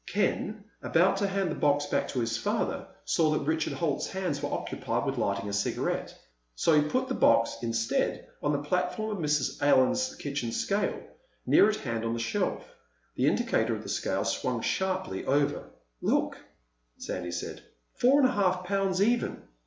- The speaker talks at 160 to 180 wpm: Yes, average, 175 wpm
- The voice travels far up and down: Yes, wide, 7.0 semitones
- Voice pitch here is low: No, medium, 160 Hz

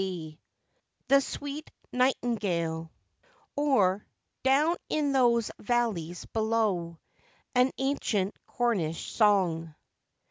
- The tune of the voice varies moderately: No, wide, 6.8 semitones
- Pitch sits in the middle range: No, high, 230 Hz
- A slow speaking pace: Yes, slow, 75 wpm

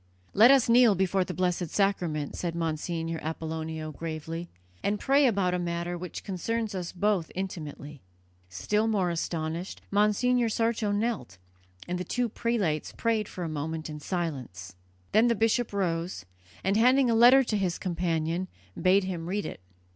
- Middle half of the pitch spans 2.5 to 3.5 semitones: No, average, 4.6 semitones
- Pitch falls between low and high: Yes, medium, 180 Hz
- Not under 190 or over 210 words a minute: No, average, 155 wpm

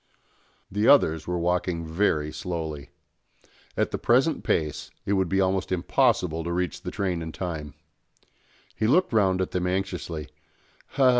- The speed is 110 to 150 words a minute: Yes, average, 145 wpm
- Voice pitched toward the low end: Yes, very low, 90 Hz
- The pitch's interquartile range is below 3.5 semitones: Yes, average, 2.9 semitones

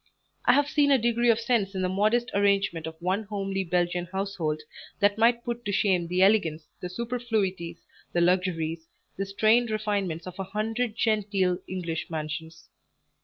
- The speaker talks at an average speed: Yes, average, 165 wpm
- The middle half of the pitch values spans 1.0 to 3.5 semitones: No, average, 3.9 semitones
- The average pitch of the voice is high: Yes, high, 195 Hz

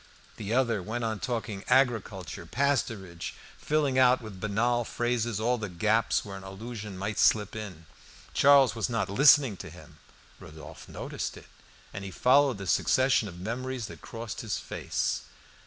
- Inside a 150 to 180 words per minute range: Yes, average, 160 wpm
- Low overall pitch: Yes, low, 110 Hz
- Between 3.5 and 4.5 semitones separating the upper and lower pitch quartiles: Yes, average, 3.9 semitones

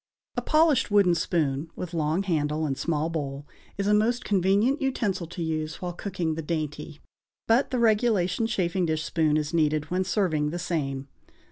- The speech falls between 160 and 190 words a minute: Yes, average, 170 wpm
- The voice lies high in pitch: No, medium, 170 Hz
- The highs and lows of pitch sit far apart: No, average, 4.5 semitones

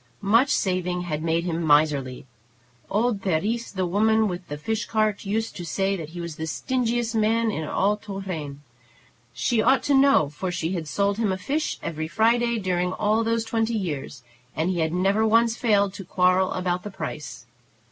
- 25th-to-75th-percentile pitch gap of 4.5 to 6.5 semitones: Yes, average, 4.9 semitones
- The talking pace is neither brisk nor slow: Yes, average, 185 wpm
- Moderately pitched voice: No, high, 195 Hz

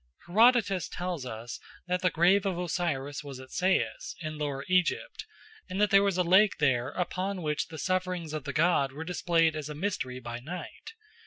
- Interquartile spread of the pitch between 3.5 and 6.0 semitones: Yes, average, 4.2 semitones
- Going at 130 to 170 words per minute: No, average, 185 wpm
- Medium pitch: Yes, medium, 170 Hz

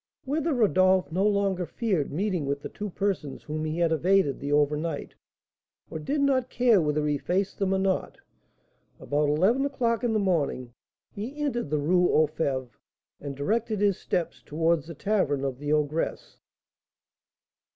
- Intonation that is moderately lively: No, wide, 5.7 semitones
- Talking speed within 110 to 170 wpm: Yes, average, 165 wpm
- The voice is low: No, medium, 175 Hz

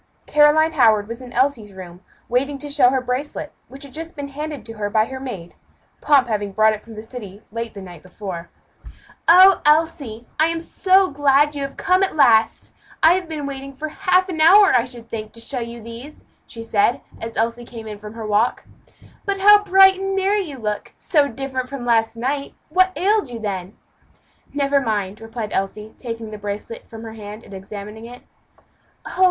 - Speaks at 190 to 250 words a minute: Yes, average, 200 wpm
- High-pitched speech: Yes, high, 245 Hz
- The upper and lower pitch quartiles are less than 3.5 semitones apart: No, wide, 5.5 semitones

